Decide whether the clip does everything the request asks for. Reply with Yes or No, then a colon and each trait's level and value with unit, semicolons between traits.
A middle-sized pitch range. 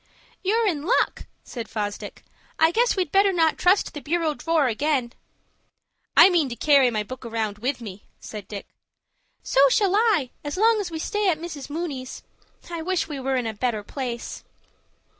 No: wide, 6.5 semitones